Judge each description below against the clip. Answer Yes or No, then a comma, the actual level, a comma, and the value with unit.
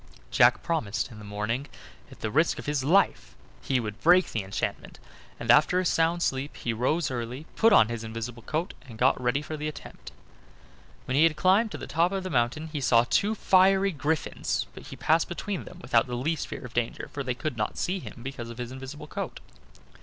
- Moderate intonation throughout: No, wide, 5.8 semitones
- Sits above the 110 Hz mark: Yes, low, 135 Hz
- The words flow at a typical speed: No, fast, 220 wpm